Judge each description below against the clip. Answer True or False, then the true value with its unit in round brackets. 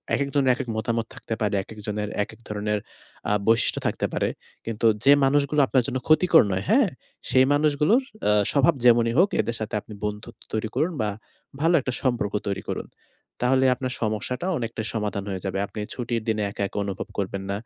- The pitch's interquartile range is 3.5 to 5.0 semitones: True (4.2 semitones)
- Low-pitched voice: True (115 Hz)